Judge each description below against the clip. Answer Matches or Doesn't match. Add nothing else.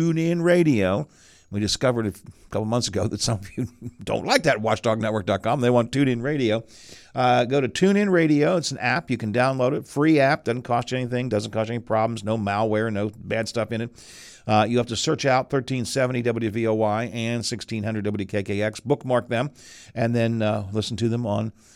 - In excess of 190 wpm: Matches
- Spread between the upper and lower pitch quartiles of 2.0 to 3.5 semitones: Matches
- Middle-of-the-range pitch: Doesn't match